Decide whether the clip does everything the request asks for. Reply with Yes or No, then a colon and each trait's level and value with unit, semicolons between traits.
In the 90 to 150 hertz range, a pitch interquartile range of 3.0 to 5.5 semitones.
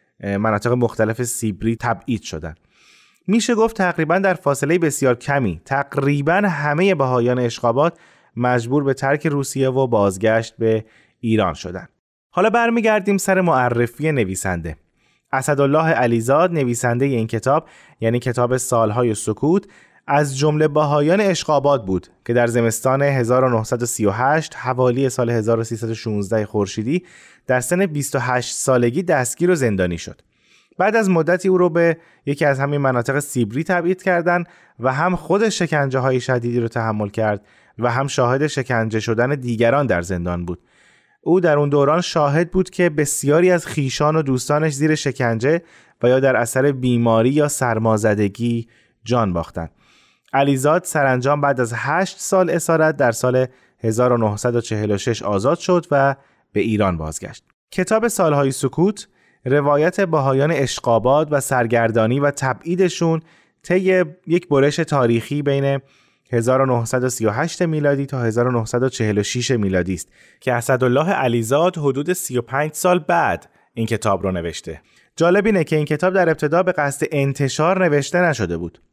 Yes: low, 135 Hz; average, 5.1 semitones